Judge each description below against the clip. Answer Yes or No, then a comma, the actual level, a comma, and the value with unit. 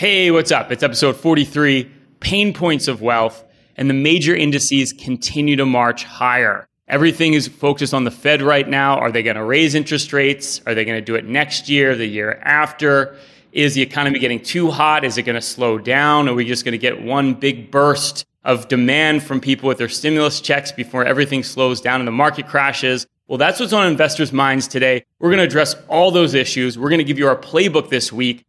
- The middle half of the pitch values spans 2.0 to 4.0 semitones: Yes, average, 3.0 semitones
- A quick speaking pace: Yes, fast, 220 wpm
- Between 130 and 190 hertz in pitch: Yes, medium, 140 Hz